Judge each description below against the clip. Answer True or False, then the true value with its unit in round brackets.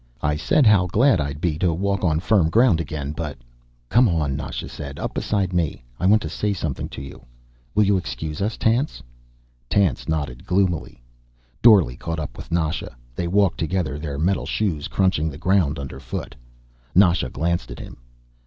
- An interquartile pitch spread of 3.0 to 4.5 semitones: False (4.9 semitones)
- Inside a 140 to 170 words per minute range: False (180 wpm)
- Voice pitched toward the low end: True (85 Hz)